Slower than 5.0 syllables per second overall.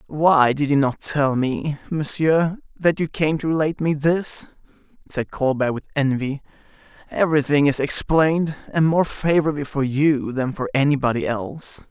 Yes: 4.8 syllables/s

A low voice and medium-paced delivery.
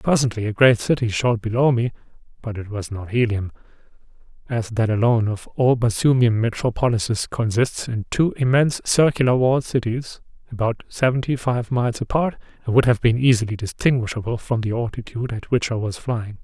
Yes: low, 120 Hz; average, 165 wpm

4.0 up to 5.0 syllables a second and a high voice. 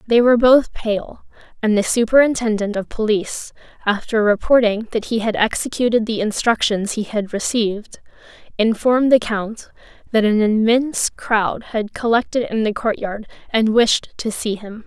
Yes: 4.8 syllables/s; high, 220 Hz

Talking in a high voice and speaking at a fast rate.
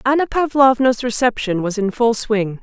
No: high, 235 Hz; average, 160 wpm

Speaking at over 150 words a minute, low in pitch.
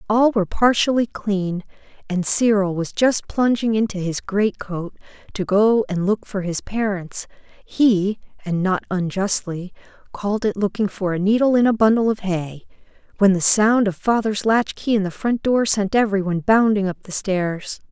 No: average, 170 wpm; high, 205 Hz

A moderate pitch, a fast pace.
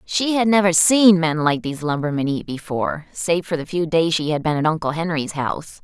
Yes: medium, 165 Hz; fast, 225 wpm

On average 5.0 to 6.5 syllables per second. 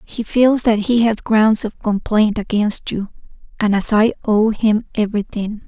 No: 4.3 syllables/s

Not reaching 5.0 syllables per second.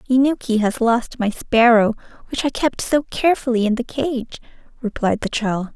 Yes: 4.8 syllables/s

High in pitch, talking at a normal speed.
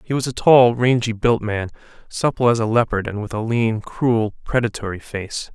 No: low, 115 Hz; average, 195 wpm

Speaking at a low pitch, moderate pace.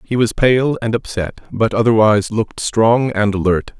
Yes: low, 115 Hz; average, 175 wpm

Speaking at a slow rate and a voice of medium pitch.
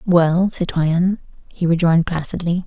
Yes: slow, 115 wpm; medium, 170 Hz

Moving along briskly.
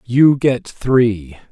No: slow, 120 wpm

